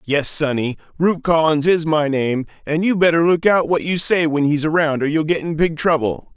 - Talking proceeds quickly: Yes, fast, 225 wpm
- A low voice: No, medium, 155 Hz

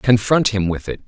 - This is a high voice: No, low, 115 Hz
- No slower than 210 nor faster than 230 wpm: Yes, fast, 225 wpm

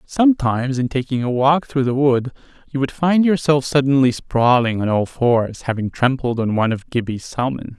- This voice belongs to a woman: No, male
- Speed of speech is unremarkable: Yes, average, 185 wpm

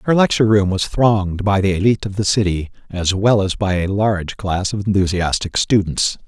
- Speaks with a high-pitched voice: No, low, 100 Hz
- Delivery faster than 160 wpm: Yes, average, 200 wpm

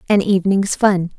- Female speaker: Yes, female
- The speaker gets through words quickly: No, average, 150 wpm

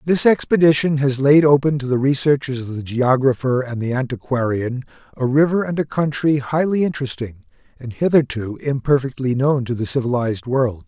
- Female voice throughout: No, male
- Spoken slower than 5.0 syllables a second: No, 5.4 syllables/s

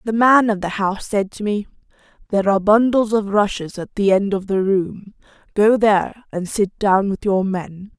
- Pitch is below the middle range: No, high, 200 Hz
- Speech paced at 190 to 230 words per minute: Yes, fast, 205 wpm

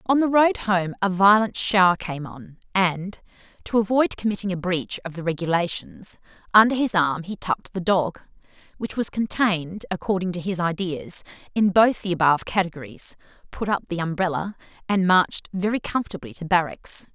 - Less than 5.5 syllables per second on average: Yes, 5.2 syllables/s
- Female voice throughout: Yes, female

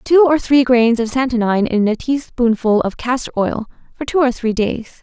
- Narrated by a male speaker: No, female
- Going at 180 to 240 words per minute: Yes, fast, 205 wpm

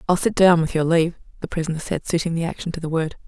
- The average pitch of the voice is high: No, medium, 165 Hz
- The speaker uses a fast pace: Yes, fast, 275 wpm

